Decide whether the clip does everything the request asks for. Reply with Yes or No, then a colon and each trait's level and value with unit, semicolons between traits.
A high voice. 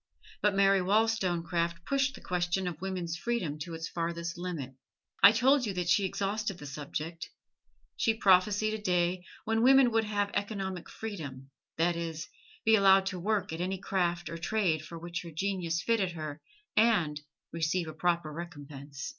No: medium, 180 Hz